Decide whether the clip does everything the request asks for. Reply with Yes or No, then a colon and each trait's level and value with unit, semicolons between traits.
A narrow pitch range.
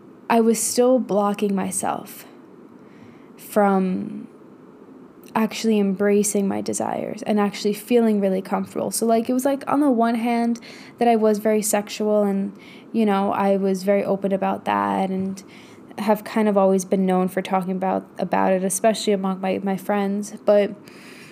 Yes: narrow, 2.2 semitones